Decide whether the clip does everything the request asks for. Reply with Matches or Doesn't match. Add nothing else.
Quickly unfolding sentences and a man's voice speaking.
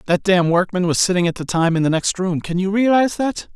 Matches